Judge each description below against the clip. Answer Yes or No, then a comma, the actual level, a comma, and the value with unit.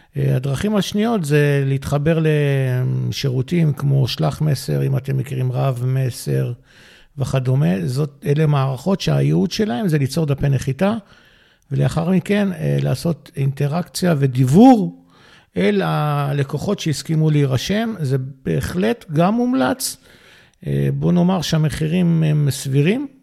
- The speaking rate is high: No, average, 105 wpm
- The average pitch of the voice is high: No, medium, 145 Hz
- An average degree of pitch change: Yes, average, 4.6 semitones